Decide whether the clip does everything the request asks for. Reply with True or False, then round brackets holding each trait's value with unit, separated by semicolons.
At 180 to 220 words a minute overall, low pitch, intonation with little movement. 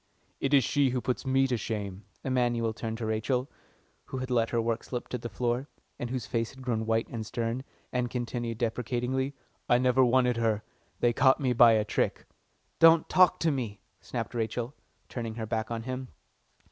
True (185 wpm; 120 Hz; 2.2 semitones)